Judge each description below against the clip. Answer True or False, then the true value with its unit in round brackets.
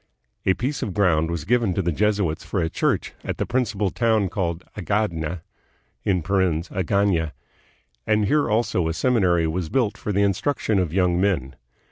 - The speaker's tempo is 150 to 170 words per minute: True (155 wpm)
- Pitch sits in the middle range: False (95 Hz)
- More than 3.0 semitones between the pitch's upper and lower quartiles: True (3.9 semitones)